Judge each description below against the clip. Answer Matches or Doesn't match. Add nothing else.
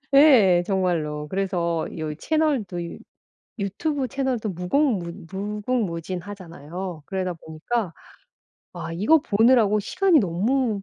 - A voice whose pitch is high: Matches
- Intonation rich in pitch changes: Matches